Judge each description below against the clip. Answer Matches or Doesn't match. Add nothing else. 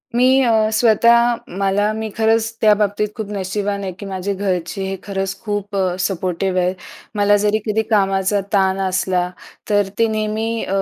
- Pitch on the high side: Matches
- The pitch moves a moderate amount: Doesn't match